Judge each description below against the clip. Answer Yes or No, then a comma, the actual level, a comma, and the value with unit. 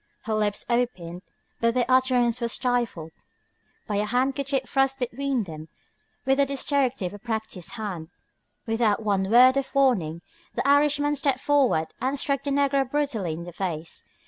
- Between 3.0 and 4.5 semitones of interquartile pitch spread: No, average, 5.0 semitones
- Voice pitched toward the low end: No, high, 245 Hz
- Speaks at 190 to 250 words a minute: No, average, 160 wpm